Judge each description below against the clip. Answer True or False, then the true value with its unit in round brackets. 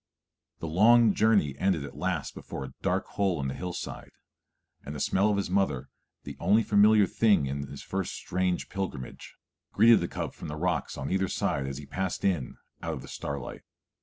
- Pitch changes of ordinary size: False (5.8 semitones)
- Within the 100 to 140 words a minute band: False (195 wpm)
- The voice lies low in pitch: True (90 Hz)